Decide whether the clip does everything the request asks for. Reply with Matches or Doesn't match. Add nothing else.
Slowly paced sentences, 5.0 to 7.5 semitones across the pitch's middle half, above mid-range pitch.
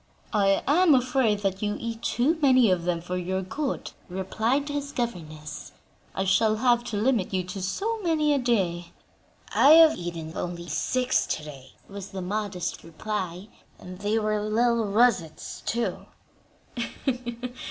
Doesn't match